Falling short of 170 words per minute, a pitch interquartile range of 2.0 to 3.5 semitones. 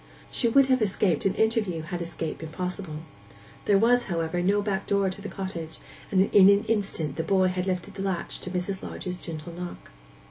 No: average, 190 wpm; average, 2.8 semitones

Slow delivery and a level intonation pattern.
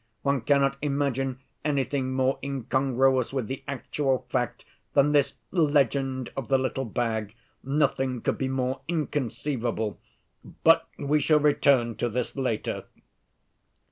Yes: slow, 125 wpm; narrow, 1.9 semitones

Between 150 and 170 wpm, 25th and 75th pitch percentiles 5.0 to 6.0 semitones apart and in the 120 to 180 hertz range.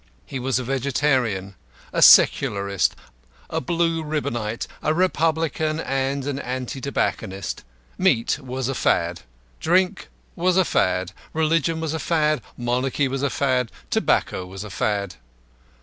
No: slow, 135 wpm; wide, 5.4 semitones; low, 135 Hz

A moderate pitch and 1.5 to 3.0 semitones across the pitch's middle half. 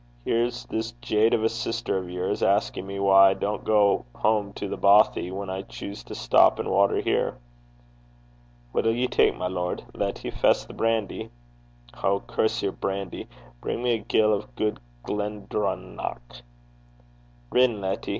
No: low, 100 Hz; narrow, 2.5 semitones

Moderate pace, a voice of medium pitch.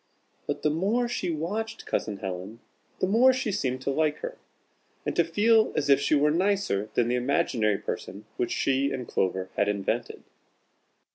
Yes: average, 170 wpm; medium, 145 Hz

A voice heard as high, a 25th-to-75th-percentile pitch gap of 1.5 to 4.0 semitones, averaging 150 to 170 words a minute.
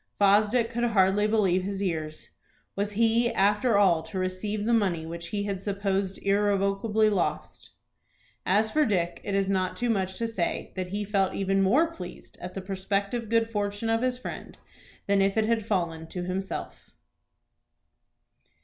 Yes: high, 200 Hz; narrow, 2.5 semitones; average, 165 wpm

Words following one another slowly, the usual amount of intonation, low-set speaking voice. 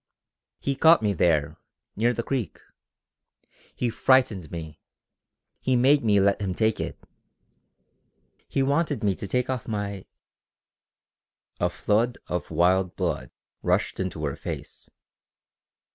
No: slow, 125 wpm; wide, 6.0 semitones; low, 105 Hz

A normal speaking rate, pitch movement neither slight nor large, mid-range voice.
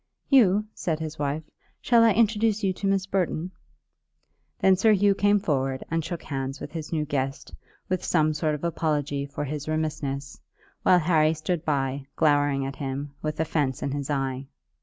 Yes: average, 175 wpm; average, 4.5 semitones; medium, 155 Hz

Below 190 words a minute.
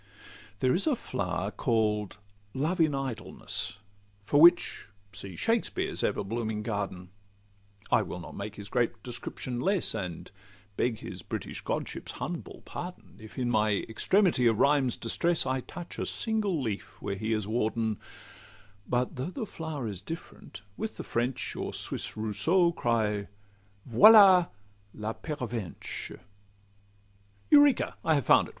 Yes: average, 140 wpm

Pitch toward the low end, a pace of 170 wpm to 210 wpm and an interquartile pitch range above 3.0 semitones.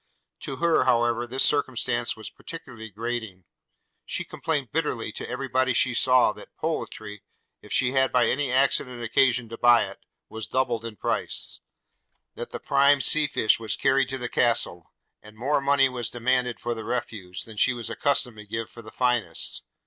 No: low, 120 Hz; average, 180 wpm; average, 2.7 semitones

